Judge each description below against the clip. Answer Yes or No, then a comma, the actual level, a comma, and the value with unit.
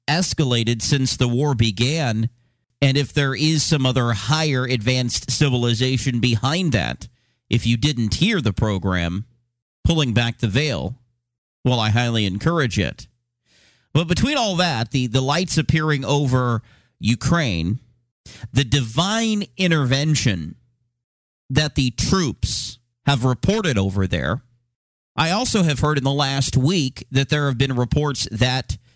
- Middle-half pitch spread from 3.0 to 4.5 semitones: Yes, average, 3.6 semitones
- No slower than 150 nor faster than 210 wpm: No, slow, 135 wpm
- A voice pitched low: Yes, low, 130 Hz